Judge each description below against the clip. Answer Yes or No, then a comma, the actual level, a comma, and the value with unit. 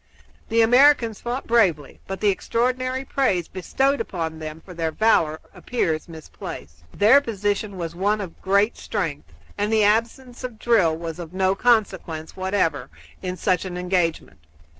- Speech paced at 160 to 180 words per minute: No, average, 150 wpm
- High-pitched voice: Yes, high, 195 Hz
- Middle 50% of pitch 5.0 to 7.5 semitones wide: Yes, wide, 5.6 semitones